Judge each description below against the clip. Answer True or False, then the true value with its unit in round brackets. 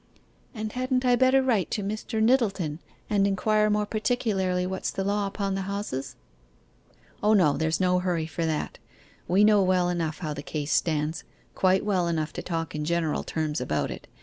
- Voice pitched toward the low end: False (190 Hz)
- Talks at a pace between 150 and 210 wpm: True (180 wpm)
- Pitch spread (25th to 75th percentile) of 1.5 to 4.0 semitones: False (4.5 semitones)